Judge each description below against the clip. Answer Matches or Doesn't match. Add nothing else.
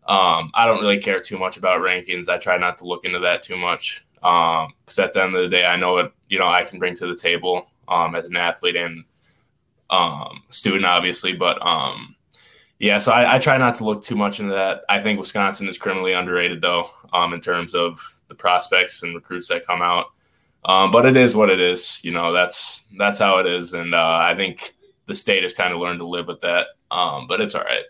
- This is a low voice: Matches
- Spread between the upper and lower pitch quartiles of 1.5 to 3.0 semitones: Matches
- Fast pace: Matches